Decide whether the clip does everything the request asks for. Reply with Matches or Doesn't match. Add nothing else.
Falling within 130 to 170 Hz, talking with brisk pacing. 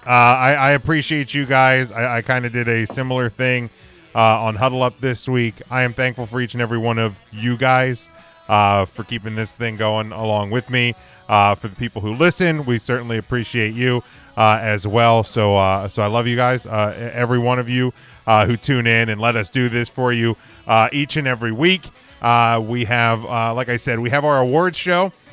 Doesn't match